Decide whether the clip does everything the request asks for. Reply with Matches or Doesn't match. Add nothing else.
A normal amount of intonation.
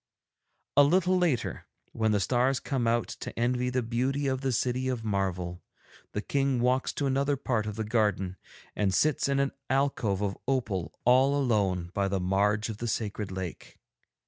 Matches